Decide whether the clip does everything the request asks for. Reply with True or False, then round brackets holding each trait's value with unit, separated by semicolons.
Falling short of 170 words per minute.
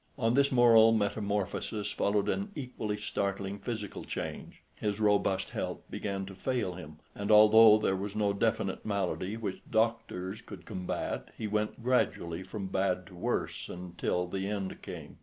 True (155 wpm)